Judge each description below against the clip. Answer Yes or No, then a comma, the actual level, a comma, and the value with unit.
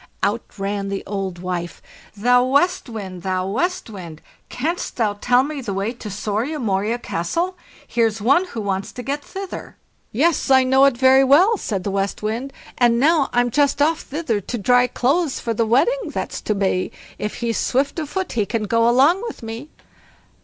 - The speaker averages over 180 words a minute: Yes, average, 190 wpm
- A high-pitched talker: Yes, high, 240 Hz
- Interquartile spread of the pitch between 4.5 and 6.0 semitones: Yes, wide, 5.6 semitones